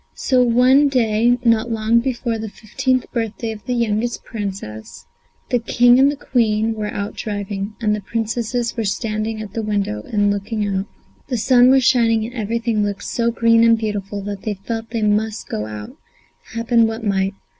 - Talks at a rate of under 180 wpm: No, average, 185 wpm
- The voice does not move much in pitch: Yes, narrow, 2.3 semitones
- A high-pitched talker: Yes, high, 225 Hz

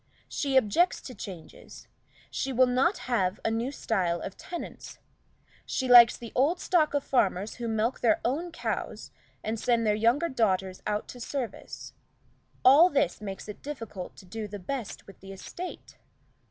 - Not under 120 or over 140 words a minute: No, average, 165 wpm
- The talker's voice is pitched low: No, high, 235 Hz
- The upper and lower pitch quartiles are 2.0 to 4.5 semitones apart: No, average, 4.9 semitones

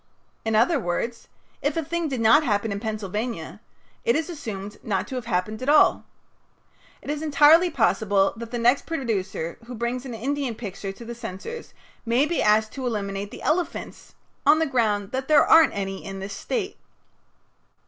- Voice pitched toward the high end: Yes, high, 235 Hz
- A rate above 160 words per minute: Yes, average, 180 wpm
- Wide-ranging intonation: Yes, wide, 5.9 semitones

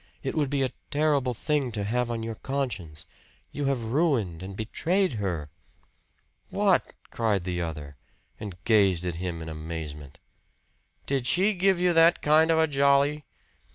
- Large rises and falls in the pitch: Yes, wide, 8.6 semitones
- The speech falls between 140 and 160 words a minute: Yes, average, 155 wpm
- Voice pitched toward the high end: No, low, 120 Hz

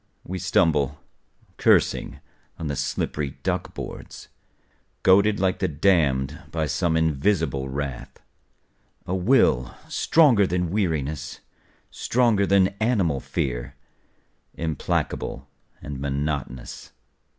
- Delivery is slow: Yes, slow, 95 wpm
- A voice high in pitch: No, very low, 80 Hz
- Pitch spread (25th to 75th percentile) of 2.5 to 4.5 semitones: No, wide, 5.4 semitones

